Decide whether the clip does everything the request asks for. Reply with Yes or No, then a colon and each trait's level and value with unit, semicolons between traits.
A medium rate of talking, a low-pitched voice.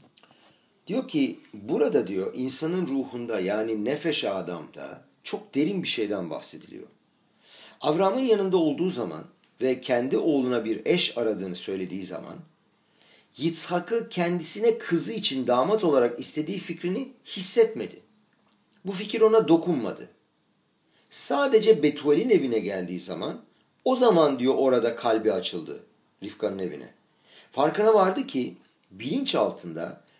No: average, 115 wpm; medium, 165 Hz